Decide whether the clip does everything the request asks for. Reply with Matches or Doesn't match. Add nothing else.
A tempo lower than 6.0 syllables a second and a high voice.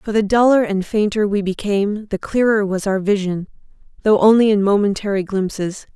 Matches